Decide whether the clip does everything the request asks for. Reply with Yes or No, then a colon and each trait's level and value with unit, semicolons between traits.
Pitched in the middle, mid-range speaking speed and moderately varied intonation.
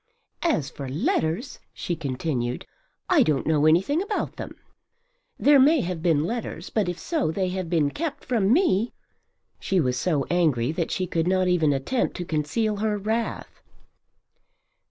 No: medium, 180 Hz; average, 155 wpm; wide, 6.2 semitones